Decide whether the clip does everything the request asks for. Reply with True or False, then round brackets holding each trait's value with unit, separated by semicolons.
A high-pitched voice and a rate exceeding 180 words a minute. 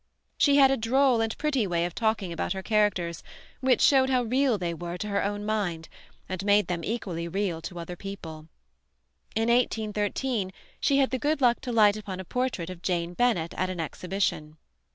True (205 Hz; 195 wpm)